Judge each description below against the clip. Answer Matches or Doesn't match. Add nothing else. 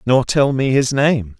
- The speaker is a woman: Doesn't match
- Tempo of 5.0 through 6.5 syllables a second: Doesn't match